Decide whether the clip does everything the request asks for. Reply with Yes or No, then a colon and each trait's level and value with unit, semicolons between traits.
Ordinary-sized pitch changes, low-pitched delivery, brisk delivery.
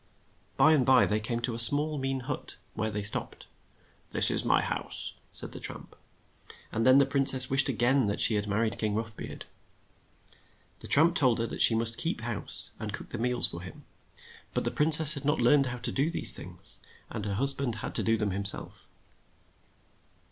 Yes: average, 4.0 semitones; low, 120 Hz; fast, 215 wpm